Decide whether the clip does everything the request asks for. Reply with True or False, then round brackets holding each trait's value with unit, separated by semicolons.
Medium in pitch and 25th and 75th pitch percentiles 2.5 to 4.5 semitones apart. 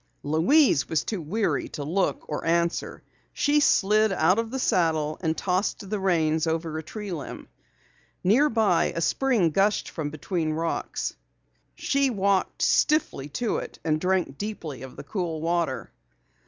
False (175 Hz; 4.9 semitones)